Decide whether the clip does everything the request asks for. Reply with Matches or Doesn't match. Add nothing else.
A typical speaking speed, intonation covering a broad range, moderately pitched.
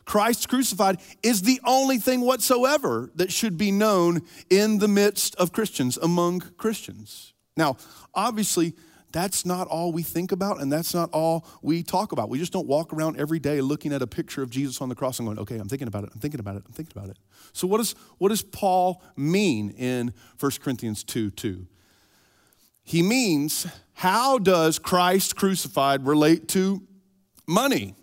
Matches